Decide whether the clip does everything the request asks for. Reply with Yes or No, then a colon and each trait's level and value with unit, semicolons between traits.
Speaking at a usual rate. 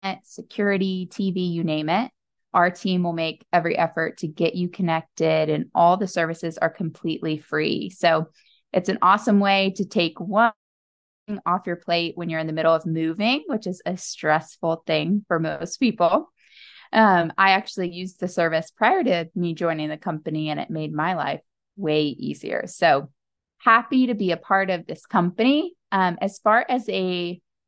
Yes: average, 180 wpm